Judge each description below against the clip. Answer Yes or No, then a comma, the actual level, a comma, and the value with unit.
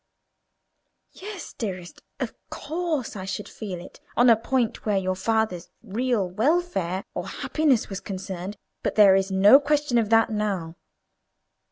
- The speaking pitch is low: No, high, 210 Hz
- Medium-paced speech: Yes, average, 145 wpm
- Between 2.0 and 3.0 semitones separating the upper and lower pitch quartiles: No, average, 4.9 semitones